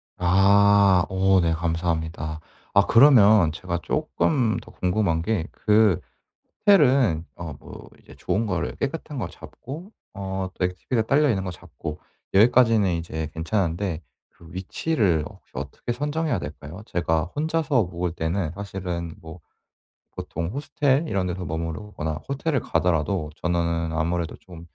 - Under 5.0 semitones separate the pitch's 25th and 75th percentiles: No, average, 5.3 semitones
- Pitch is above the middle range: No, very low, 95 Hz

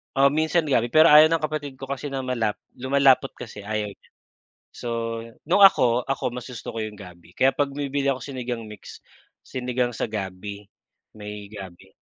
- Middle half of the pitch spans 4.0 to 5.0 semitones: Yes, average, 4.7 semitones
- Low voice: Yes, low, 125 Hz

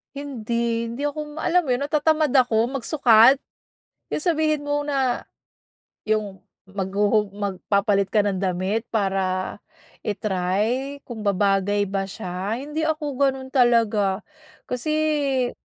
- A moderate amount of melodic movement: No, wide, 6.1 semitones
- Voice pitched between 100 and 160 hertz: No, high, 230 Hz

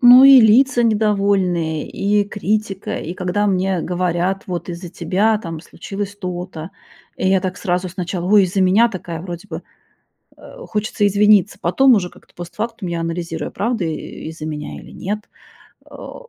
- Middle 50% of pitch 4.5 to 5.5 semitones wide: No, average, 3.1 semitones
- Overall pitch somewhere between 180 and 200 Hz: Yes, high, 190 Hz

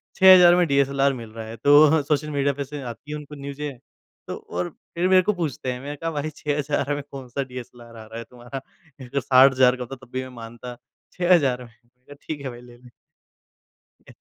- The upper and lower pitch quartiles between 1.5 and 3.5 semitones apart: Yes, average, 3.1 semitones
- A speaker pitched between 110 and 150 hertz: Yes, low, 135 Hz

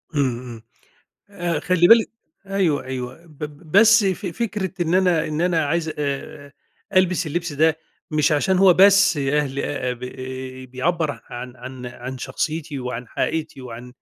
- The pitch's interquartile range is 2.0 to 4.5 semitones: No, average, 5.0 semitones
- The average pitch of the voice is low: No, medium, 155 Hz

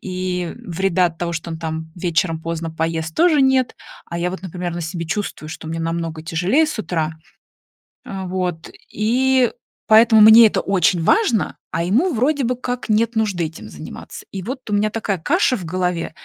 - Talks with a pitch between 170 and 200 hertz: Yes, medium, 185 Hz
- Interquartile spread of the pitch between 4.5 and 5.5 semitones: Yes, average, 5.1 semitones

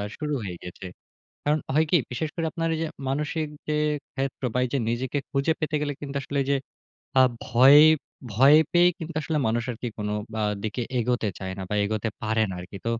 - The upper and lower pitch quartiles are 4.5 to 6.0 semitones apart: Yes, average, 5.3 semitones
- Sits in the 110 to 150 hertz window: Yes, low, 135 Hz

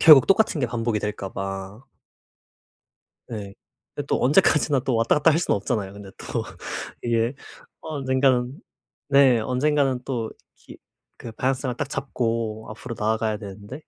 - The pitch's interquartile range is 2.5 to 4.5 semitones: Yes, average, 3.9 semitones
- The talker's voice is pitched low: Yes, low, 120 Hz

